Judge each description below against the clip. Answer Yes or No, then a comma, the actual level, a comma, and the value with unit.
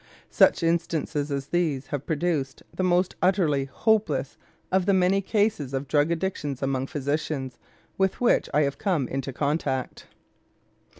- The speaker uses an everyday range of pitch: Yes, average, 4.7 semitones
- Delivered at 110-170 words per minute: Yes, average, 140 wpm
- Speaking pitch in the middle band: Yes, medium, 150 Hz